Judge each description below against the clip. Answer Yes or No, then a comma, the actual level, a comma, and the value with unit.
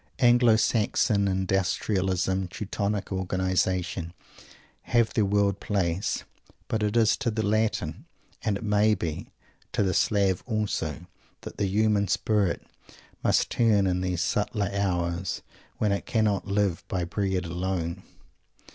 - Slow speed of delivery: Yes, slow, 130 wpm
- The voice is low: Yes, low, 100 Hz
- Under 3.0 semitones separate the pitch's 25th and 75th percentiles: Yes, narrow, 2.4 semitones